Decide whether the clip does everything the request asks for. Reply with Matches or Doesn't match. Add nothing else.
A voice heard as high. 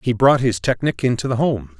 Doesn't match